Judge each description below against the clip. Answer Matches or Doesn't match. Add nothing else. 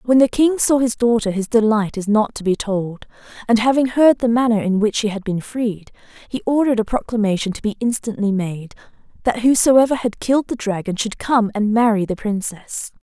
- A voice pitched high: Matches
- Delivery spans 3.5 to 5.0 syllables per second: Doesn't match